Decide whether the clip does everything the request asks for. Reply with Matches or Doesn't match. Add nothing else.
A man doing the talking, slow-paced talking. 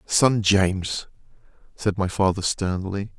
Matches